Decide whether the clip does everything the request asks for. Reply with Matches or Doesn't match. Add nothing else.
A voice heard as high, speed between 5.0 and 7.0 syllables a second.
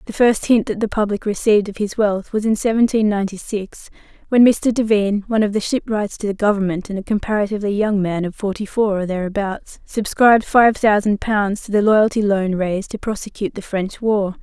Matches